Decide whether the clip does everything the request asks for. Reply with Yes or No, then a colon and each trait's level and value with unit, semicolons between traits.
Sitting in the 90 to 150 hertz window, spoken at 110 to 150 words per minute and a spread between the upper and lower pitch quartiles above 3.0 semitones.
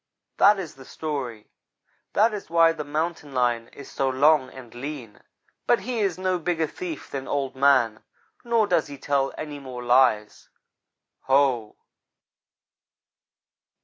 Yes: medium, 140 Hz; average, 140 wpm; average, 4.4 semitones